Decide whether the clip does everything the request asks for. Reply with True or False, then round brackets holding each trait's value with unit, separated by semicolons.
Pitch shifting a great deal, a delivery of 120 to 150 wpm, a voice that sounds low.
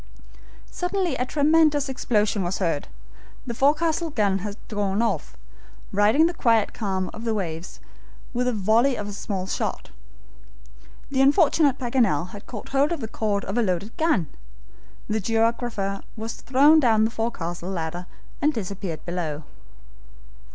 False (5.7 semitones; 145 wpm; 220 Hz)